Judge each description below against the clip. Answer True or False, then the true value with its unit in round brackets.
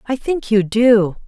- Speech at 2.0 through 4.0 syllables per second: True (3.7 syllables/s)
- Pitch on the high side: True (225 Hz)